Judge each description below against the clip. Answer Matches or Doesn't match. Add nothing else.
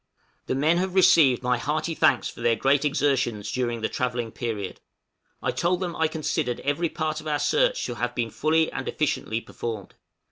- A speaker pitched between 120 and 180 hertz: Matches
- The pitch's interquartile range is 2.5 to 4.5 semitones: Doesn't match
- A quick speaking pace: Doesn't match